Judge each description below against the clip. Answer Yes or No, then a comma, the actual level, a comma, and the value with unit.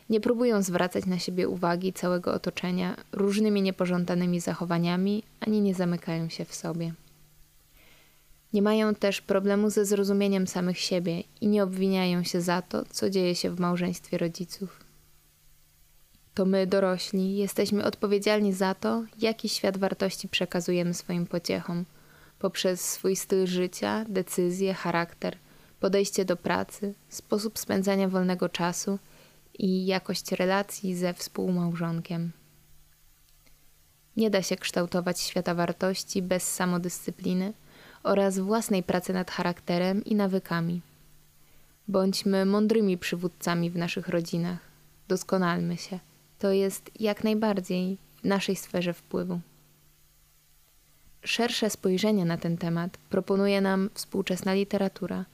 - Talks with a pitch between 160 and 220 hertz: Yes, medium, 185 Hz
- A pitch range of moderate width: No, narrow, 2.3 semitones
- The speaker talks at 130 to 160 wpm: No, average, 115 wpm